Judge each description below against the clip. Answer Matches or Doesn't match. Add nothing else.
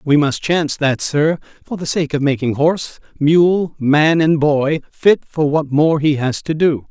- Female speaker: Doesn't match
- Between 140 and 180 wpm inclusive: Doesn't match